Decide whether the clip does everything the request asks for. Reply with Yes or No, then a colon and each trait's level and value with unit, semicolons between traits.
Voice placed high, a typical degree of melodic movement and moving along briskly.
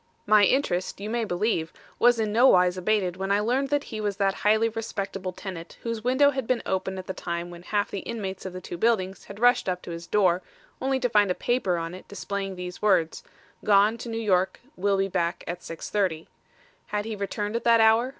Yes: high, 200 Hz; average, 3.6 semitones; fast, 220 wpm